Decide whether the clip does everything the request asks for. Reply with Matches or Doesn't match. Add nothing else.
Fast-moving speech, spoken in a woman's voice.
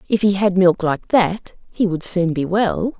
Matches